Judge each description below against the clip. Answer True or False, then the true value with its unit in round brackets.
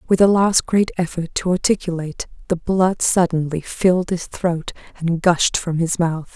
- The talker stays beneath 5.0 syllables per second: True (4.6 syllables/s)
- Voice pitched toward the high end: False (175 Hz)